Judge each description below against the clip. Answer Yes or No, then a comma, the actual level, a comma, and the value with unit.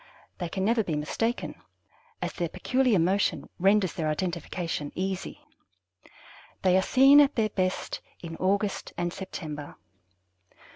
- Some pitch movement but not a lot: Yes, average, 3.8 semitones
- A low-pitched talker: No, medium, 185 Hz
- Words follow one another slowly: Yes, slow, 130 wpm